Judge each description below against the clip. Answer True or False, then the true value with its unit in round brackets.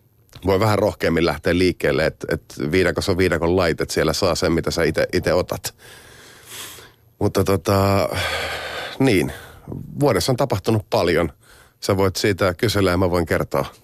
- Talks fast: False (145 wpm)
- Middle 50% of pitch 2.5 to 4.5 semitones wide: True (3.8 semitones)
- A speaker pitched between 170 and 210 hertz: False (100 Hz)